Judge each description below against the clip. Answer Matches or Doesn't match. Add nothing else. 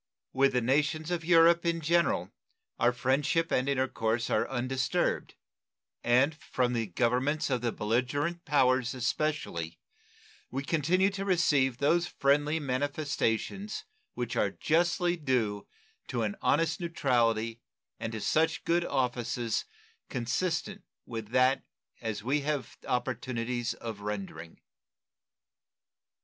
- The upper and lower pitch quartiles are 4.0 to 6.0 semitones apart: Matches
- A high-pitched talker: Doesn't match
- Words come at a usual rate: Doesn't match